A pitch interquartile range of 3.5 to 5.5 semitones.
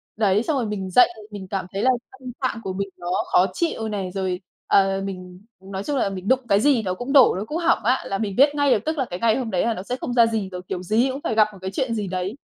Yes: average, 4.7 semitones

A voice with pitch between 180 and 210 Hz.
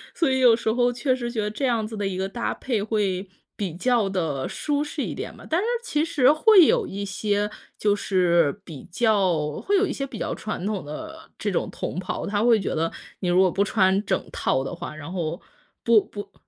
Yes: high, 205 Hz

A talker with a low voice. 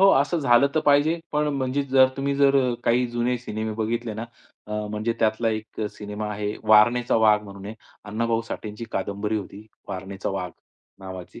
Yes: low, 110 Hz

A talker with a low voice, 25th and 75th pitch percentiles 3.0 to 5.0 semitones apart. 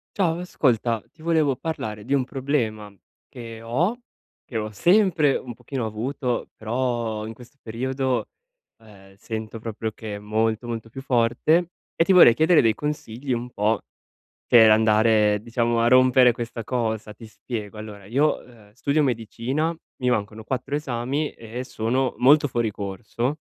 Yes: low, 120 Hz; average, 3.4 semitones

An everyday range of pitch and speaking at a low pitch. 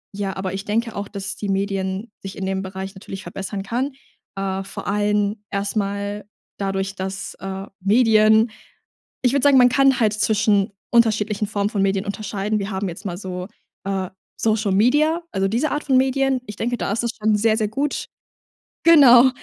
No: average, 3.1 semitones; high, 205 Hz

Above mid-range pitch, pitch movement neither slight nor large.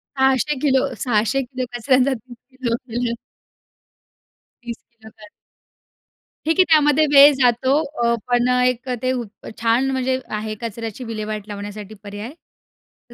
Yes: high, 245 Hz; average, 3.0 semitones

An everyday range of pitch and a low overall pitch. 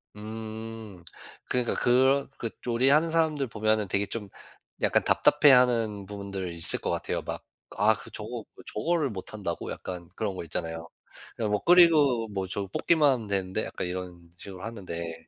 Yes: average, 5.0 semitones; low, 110 Hz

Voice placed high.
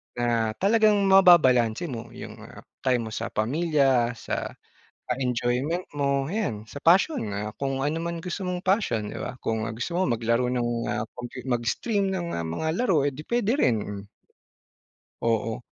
No: low, 135 Hz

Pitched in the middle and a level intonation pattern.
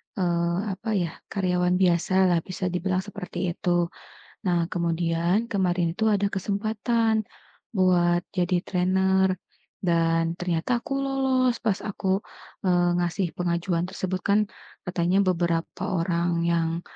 Yes: medium, 180 Hz; narrow, 2.2 semitones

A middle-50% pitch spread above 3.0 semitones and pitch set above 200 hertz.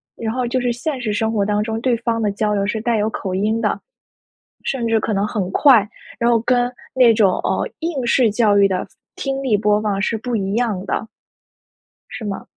No: average, 2.7 semitones; high, 225 Hz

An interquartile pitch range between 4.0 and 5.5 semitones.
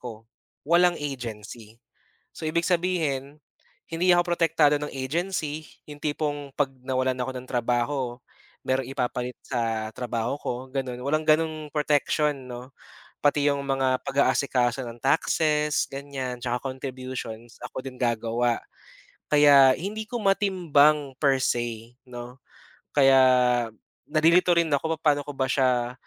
No: average, 3.6 semitones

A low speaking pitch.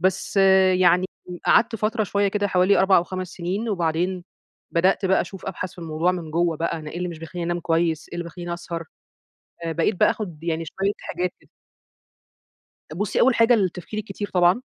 No: medium, 180 Hz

